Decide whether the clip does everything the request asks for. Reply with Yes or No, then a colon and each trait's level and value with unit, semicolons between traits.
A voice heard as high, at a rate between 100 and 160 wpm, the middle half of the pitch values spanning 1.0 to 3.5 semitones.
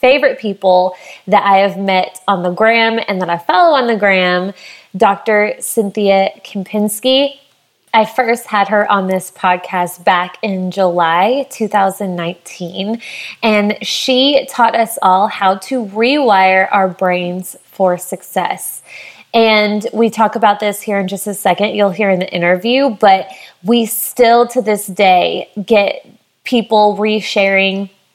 Yes: high, 205 Hz; average, 140 wpm; average, 3.2 semitones